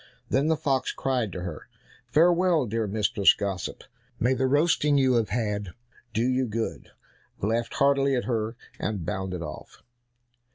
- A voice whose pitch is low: Yes, low, 115 Hz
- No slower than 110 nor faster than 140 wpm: No, average, 150 wpm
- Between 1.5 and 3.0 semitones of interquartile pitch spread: No, average, 4.9 semitones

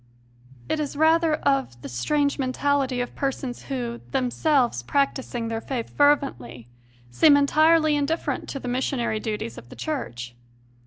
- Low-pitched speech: No, very high, 270 Hz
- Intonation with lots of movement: No, average, 3.9 semitones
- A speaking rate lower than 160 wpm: Yes, average, 140 wpm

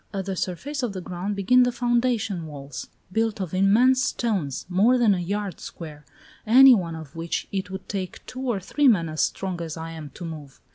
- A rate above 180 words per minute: Yes, fast, 205 wpm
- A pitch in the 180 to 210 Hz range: Yes, high, 190 Hz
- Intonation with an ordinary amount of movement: No, wide, 5.9 semitones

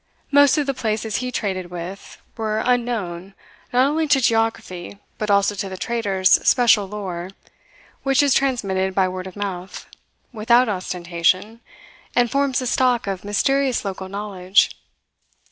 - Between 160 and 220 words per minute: No, average, 145 wpm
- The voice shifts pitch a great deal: No, average, 4.6 semitones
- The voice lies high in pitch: Yes, high, 210 Hz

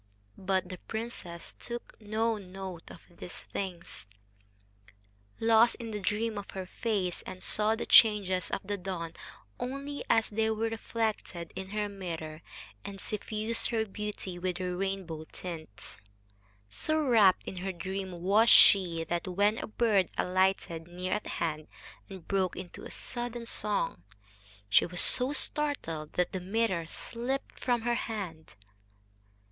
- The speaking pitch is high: Yes, high, 195 Hz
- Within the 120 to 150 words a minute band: Yes, average, 140 wpm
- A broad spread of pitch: No, average, 3.8 semitones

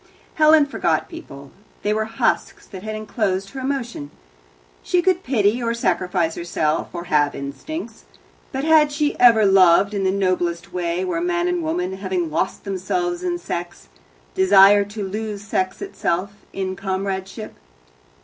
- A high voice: Yes, high, 195 Hz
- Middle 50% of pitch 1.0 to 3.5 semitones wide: No, average, 4.7 semitones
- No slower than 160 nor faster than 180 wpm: No, average, 150 wpm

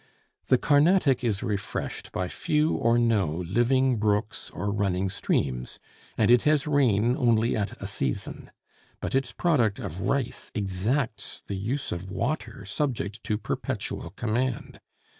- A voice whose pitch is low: Yes, low, 115 Hz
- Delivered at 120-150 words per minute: Yes, average, 140 wpm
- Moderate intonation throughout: Yes, average, 4.8 semitones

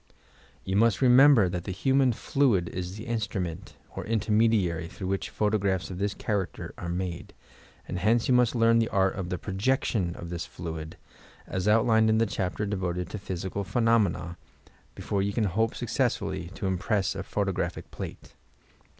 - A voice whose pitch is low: Yes, low, 100 Hz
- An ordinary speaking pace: Yes, average, 165 wpm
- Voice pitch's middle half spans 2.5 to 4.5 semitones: Yes, average, 3.8 semitones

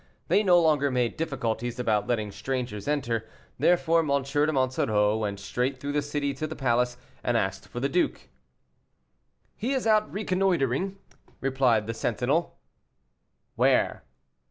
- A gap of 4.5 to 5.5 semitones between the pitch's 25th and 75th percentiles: Yes, average, 4.9 semitones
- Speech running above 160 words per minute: No, average, 140 wpm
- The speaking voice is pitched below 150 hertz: Yes, low, 135 Hz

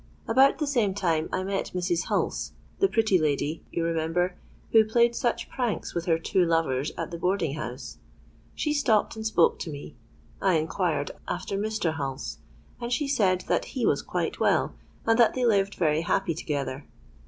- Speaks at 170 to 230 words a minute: Yes, average, 175 wpm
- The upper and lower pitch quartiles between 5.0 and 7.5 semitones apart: Yes, wide, 5.5 semitones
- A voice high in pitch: No, medium, 180 Hz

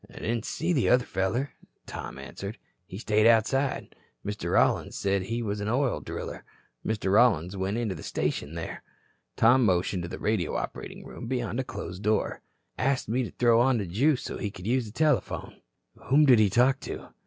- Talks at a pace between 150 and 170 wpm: No, average, 190 wpm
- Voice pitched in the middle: No, low, 110 Hz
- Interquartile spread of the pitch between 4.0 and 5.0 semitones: Yes, average, 4.3 semitones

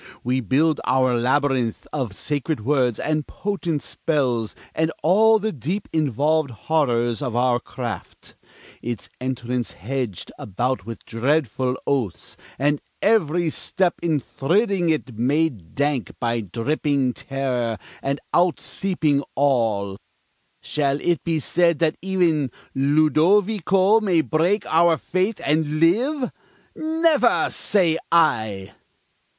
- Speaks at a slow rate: Yes, slow, 115 wpm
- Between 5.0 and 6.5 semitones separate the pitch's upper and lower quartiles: Yes, average, 5.3 semitones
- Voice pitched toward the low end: No, medium, 145 Hz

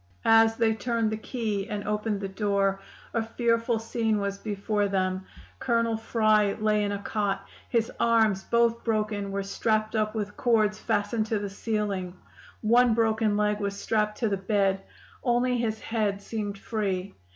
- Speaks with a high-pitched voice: Yes, high, 215 Hz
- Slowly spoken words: No, average, 165 wpm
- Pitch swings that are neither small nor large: No, narrow, 2.0 semitones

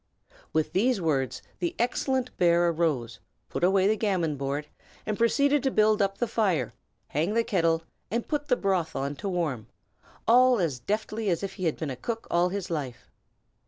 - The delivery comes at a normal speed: Yes, average, 185 wpm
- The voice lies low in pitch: No, medium, 185 Hz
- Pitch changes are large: Yes, wide, 5.7 semitones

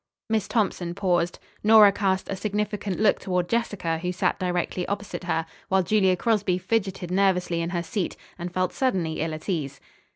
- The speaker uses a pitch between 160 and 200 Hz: Yes, medium, 185 Hz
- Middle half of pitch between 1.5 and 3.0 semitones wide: Yes, average, 2.7 semitones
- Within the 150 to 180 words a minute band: Yes, average, 170 wpm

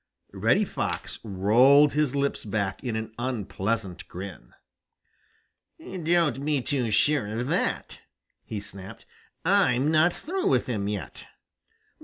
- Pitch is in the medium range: No, low, 125 Hz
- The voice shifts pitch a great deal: Yes, wide, 6.5 semitones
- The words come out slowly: Yes, slow, 130 wpm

